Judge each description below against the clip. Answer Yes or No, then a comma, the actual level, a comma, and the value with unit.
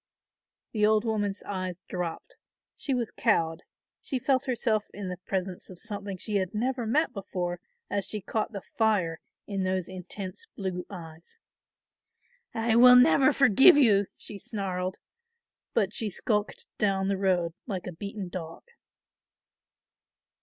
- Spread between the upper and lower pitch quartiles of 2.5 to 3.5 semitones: Yes, average, 3.2 semitones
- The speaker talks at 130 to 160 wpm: Yes, average, 140 wpm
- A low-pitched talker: No, high, 200 Hz